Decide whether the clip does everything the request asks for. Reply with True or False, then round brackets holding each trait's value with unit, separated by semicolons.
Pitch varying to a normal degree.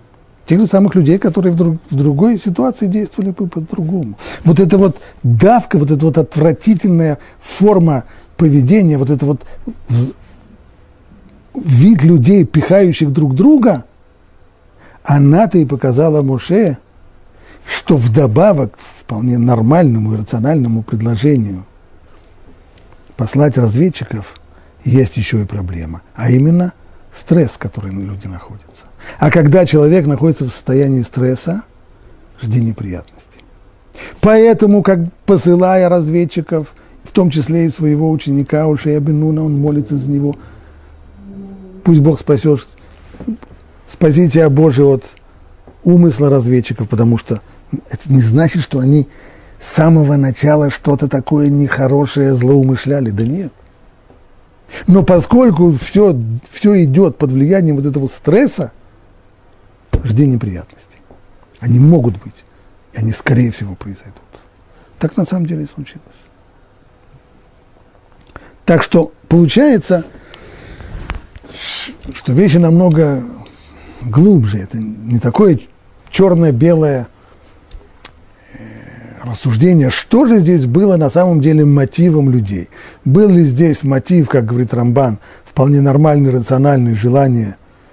False (7.2 semitones)